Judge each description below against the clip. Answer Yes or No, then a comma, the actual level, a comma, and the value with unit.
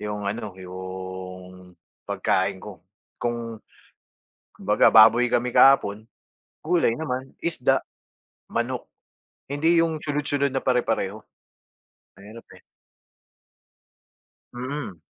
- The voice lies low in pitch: Yes, low, 115 Hz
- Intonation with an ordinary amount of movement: No, wide, 6.0 semitones